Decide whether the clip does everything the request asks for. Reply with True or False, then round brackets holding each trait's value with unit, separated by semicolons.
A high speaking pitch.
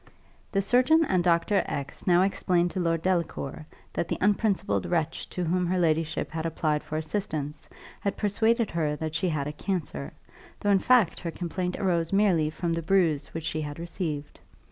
False (170 Hz)